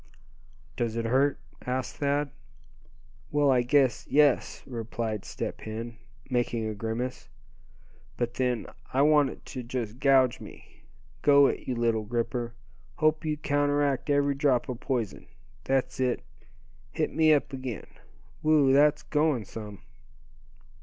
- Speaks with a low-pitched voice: Yes, low, 130 Hz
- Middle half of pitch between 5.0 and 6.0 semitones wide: No, average, 3.4 semitones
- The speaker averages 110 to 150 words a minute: Yes, slow, 135 wpm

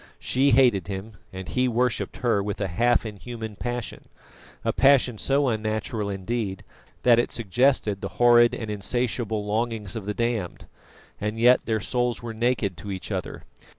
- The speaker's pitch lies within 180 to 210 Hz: No, low, 115 Hz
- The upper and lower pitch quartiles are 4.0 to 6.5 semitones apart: No, average, 2.9 semitones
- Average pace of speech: Yes, average, 160 wpm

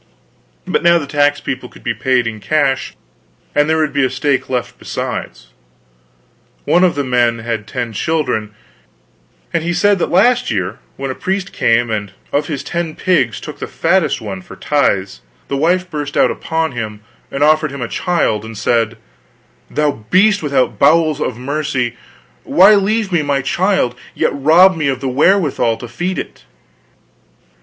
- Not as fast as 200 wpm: Yes, average, 170 wpm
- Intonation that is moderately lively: No, wide, 5.9 semitones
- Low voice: No, medium, 145 Hz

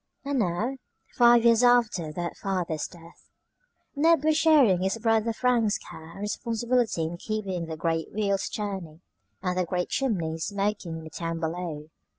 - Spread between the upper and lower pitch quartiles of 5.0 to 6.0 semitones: Yes, wide, 5.6 semitones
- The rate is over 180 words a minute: No, average, 160 wpm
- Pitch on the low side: No, high, 195 Hz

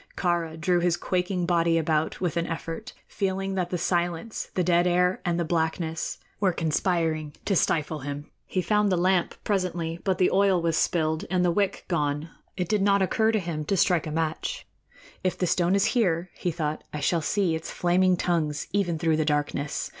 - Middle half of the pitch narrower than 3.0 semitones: Yes, narrow, 2.5 semitones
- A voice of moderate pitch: Yes, medium, 175 Hz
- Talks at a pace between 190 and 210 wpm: Yes, average, 195 wpm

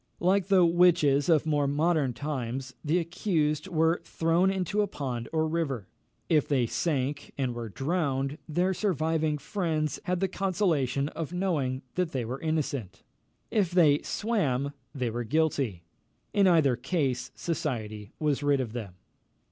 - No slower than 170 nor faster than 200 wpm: No, average, 150 wpm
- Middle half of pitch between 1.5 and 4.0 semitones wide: No, average, 4.6 semitones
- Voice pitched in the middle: Yes, medium, 150 Hz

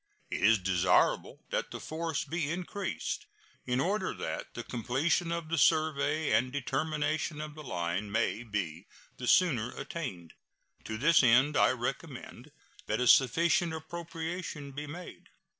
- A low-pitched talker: No, medium, 145 Hz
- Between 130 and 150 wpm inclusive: Yes, average, 140 wpm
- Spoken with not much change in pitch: No, wide, 5.5 semitones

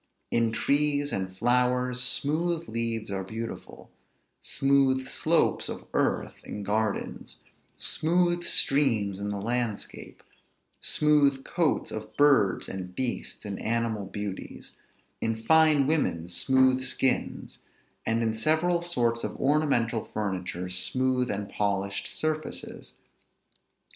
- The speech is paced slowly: Yes, slow, 110 wpm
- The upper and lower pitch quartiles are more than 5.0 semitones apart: Yes, wide, 5.6 semitones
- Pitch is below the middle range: Yes, low, 120 Hz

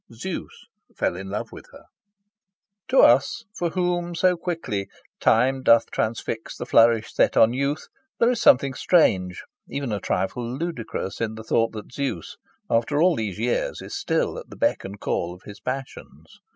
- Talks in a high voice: No, low, 120 Hz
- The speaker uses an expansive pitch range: Yes, wide, 6.9 semitones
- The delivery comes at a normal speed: Yes, average, 170 wpm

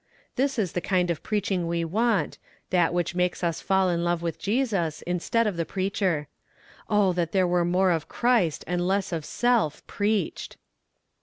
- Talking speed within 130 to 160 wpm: No, average, 175 wpm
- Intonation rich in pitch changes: No, average, 3.0 semitones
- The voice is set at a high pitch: No, medium, 180 Hz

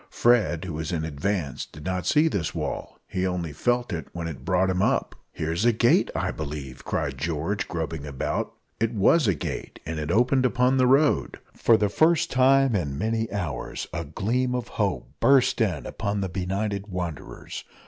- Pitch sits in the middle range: No, very low, 95 Hz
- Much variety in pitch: Yes, wide, 6.9 semitones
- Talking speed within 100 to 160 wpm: No, average, 185 wpm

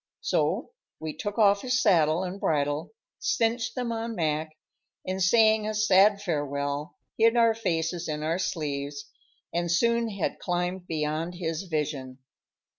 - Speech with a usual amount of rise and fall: No, wide, 5.7 semitones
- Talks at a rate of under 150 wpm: Yes, average, 140 wpm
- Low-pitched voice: No, medium, 175 Hz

